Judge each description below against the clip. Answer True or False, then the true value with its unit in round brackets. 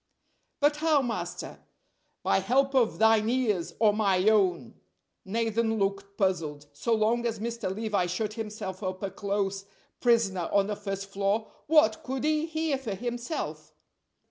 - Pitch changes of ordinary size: True (3.3 semitones)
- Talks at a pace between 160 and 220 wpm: False (145 wpm)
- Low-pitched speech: False (215 Hz)